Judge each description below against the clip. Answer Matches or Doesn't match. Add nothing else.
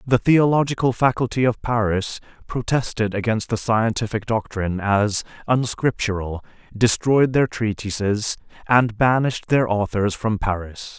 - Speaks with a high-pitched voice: Doesn't match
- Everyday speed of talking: Doesn't match